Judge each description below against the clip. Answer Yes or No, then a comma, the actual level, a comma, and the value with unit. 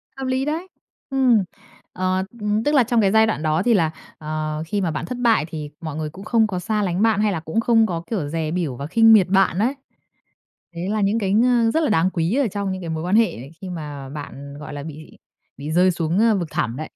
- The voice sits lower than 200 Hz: Yes, medium, 185 Hz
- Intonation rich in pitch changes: Yes, wide, 6.0 semitones